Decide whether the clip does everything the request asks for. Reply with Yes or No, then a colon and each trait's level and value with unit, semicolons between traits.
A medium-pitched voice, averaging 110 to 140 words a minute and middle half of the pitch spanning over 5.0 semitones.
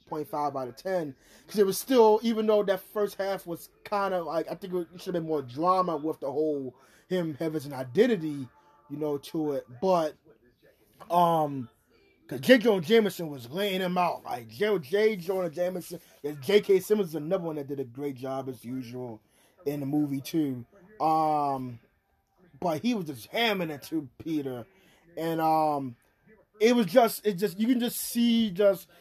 No: medium, 165 Hz; average, 180 wpm; wide, 5.6 semitones